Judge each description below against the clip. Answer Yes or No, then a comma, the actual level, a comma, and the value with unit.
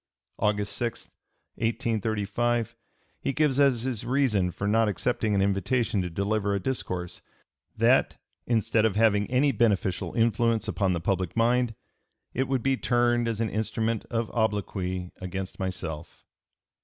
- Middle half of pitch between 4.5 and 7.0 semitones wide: No, average, 3.2 semitones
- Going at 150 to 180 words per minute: No, average, 140 wpm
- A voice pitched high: No, low, 110 Hz